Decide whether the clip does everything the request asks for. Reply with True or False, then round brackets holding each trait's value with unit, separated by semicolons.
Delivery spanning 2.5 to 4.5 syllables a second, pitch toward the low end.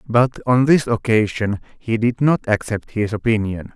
True (4.3 syllables/s; 115 Hz)